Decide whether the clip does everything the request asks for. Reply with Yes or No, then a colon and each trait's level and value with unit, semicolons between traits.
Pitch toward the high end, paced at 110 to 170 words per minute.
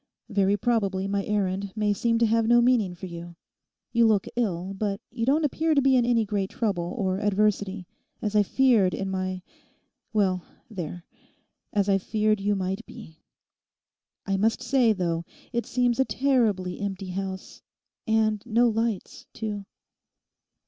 Yes: high, 205 Hz; average, 150 wpm